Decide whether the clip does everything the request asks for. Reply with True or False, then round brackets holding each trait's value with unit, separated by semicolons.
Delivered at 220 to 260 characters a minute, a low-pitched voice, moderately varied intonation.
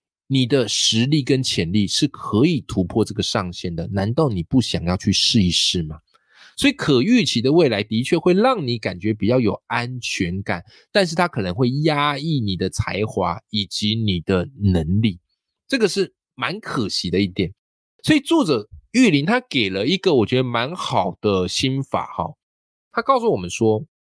False (255 characters per minute; 110 Hz; 6.7 semitones)